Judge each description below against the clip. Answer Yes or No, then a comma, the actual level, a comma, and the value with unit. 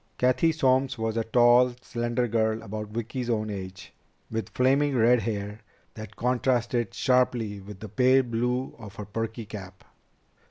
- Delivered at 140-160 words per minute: Yes, average, 150 wpm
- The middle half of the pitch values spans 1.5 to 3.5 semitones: Yes, average, 2.7 semitones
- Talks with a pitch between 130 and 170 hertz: No, low, 115 Hz